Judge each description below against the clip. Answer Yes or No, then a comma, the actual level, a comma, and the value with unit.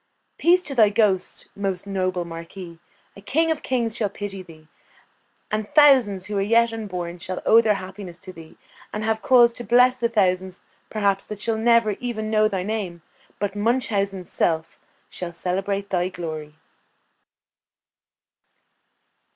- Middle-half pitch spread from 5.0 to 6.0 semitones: No, average, 3.6 semitones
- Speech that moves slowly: No, average, 150 wpm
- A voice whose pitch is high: Yes, high, 200 Hz